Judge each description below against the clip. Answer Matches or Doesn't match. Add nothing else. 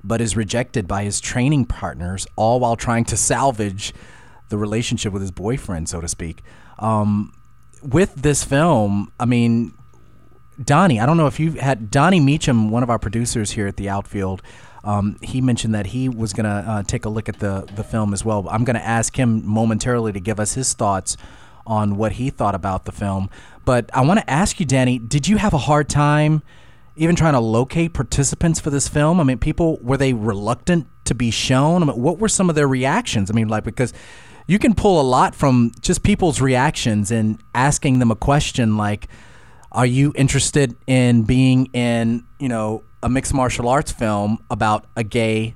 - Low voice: Matches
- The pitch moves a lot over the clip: Doesn't match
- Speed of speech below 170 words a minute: Doesn't match